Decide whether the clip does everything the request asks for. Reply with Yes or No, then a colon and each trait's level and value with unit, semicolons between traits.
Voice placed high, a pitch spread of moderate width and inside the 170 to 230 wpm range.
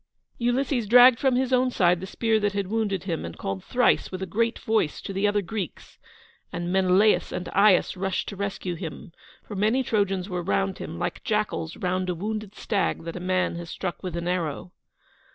Yes: high, 195 Hz; average, 3.3 semitones; average, 200 wpm